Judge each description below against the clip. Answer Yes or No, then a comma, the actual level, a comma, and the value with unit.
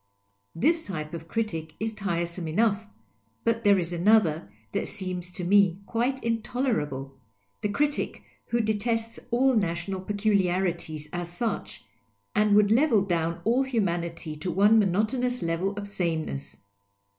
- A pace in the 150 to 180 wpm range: No, slow, 135 wpm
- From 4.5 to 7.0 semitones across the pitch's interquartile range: Yes, average, 4.8 semitones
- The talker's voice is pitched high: Yes, high, 200 Hz